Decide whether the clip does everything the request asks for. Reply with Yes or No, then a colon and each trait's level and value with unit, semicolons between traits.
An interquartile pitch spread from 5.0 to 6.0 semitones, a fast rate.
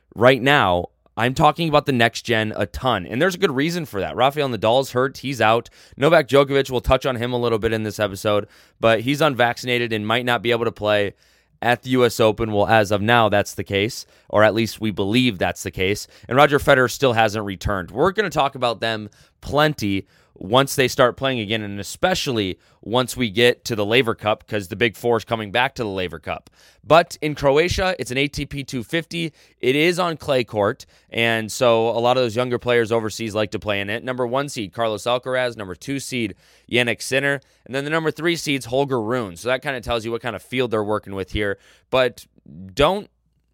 No: average, 4.0 semitones; fast, 220 wpm